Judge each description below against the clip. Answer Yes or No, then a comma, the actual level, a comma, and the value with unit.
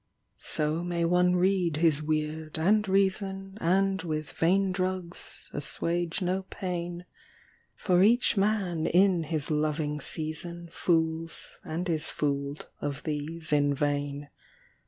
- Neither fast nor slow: No, slow, 120 wpm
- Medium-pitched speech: Yes, medium, 170 Hz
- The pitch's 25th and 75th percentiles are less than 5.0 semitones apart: Yes, average, 3.2 semitones